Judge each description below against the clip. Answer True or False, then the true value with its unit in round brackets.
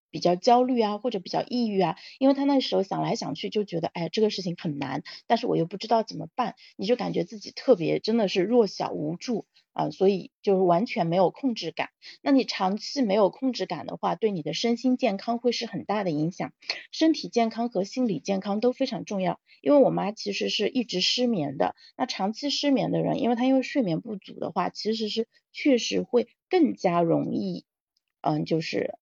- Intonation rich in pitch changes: False (5.0 semitones)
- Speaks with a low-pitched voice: False (220 Hz)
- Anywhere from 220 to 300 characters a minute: False (315 characters per minute)